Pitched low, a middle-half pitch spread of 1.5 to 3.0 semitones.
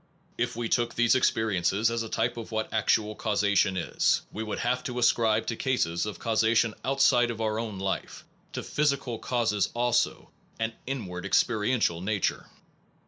Yes: low, 110 Hz; narrow, 2.4 semitones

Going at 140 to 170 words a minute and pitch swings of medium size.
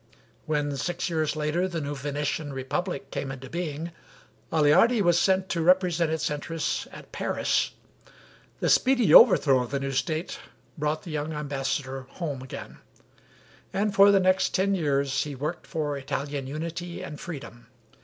Yes: average, 155 wpm; average, 3.8 semitones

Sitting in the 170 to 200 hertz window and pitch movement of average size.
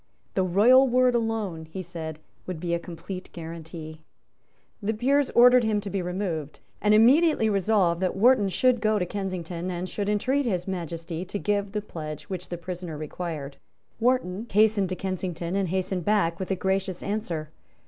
Yes: high, 190 Hz; average, 3.9 semitones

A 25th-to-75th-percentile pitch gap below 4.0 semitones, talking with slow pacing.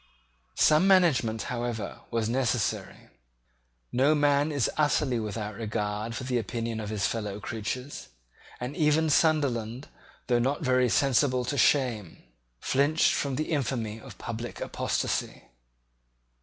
No: average, 4.3 semitones; slow, 125 wpm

